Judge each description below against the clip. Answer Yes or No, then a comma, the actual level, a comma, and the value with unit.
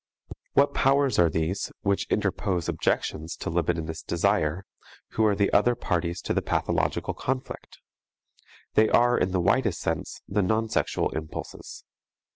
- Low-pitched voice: Yes, very low, 95 Hz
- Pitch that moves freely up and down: No, average, 4.6 semitones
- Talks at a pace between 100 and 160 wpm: Yes, average, 140 wpm